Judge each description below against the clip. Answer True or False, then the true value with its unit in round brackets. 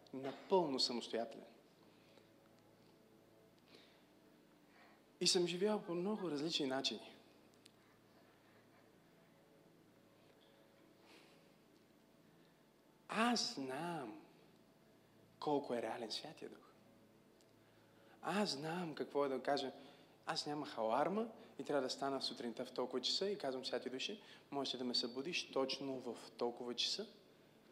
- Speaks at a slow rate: True (95 wpm)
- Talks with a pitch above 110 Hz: True (135 Hz)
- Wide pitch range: True (6.0 semitones)